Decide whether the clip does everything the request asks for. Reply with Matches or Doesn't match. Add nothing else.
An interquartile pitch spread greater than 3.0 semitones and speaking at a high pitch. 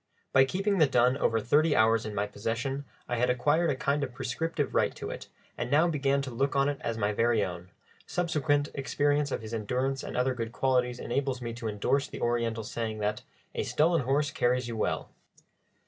Doesn't match